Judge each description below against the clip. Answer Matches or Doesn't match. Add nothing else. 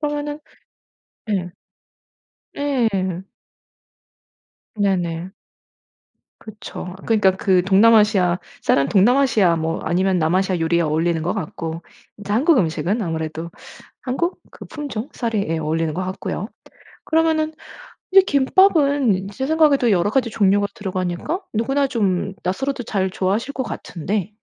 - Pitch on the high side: Matches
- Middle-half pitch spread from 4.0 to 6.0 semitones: Doesn't match